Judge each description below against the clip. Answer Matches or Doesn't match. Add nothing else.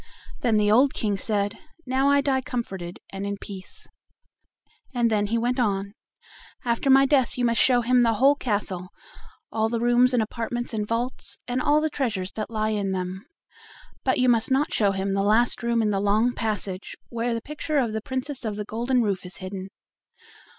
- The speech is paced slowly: Doesn't match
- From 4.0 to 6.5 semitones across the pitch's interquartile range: Doesn't match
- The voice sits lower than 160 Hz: Doesn't match